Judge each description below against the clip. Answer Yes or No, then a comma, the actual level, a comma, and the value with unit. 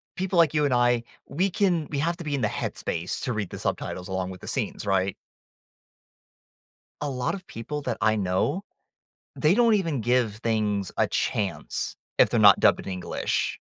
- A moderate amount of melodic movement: No, wide, 7.8 semitones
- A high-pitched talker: No, low, 120 Hz